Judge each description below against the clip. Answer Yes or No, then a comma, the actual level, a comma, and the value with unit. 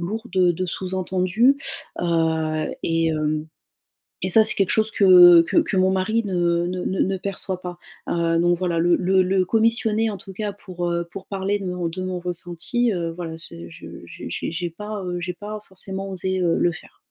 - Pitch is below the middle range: No, medium, 185 Hz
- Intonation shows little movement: Yes, narrow, 2.3 semitones